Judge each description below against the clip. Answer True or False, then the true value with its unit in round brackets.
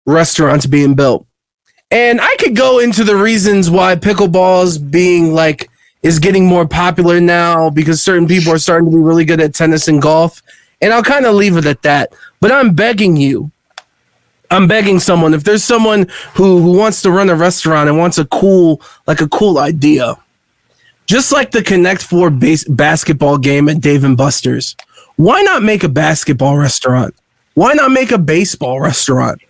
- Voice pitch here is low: False (170 Hz)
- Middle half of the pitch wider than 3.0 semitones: True (4.1 semitones)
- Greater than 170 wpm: True (180 wpm)